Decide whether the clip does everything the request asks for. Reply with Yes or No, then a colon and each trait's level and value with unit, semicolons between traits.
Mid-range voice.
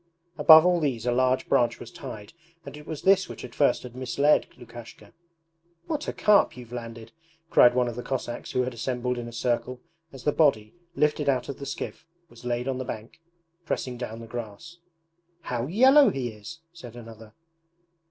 No: low, 125 Hz